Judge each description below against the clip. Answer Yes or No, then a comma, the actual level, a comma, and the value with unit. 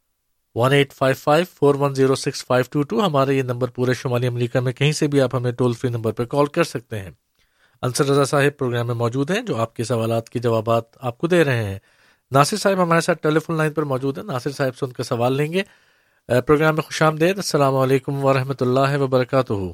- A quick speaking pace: Yes, fast, 230 wpm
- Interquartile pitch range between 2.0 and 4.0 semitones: Yes, average, 3.2 semitones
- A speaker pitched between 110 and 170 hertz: Yes, low, 135 Hz